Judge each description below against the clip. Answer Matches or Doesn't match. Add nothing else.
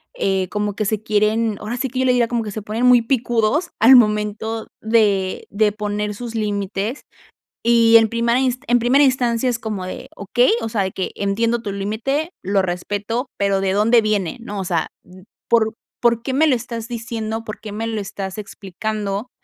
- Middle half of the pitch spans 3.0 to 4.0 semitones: Doesn't match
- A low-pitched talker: Doesn't match